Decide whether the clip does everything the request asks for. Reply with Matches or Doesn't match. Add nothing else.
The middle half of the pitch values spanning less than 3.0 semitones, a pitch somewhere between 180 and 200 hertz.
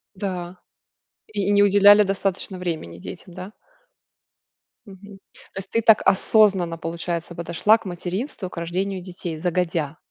Matches